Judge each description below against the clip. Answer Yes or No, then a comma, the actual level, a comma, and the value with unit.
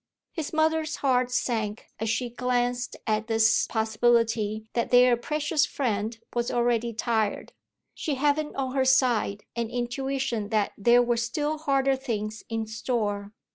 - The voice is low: No, high, 240 Hz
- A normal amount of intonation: Yes, average, 3.2 semitones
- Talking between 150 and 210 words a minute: No, average, 140 wpm